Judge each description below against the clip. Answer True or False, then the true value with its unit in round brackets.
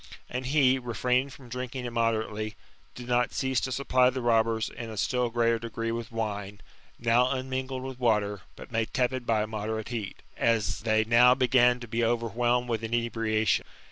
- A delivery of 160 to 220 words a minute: True (175 wpm)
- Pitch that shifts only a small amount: True (2.0 semitones)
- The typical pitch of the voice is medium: False (120 Hz)